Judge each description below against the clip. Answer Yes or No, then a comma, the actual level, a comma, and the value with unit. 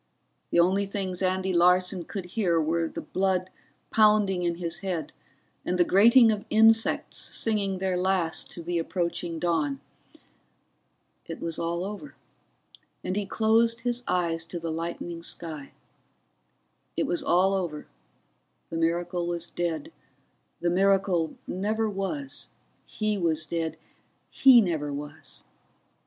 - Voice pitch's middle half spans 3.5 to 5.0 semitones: No, average, 3.0 semitones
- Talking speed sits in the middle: No, slow, 130 wpm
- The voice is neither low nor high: Yes, medium, 180 Hz